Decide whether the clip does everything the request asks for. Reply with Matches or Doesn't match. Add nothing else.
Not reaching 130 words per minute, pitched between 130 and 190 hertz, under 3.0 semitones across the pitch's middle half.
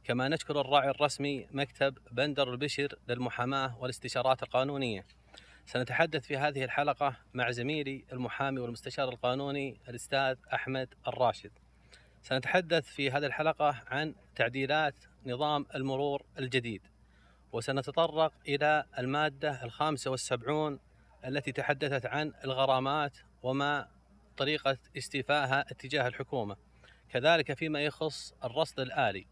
Matches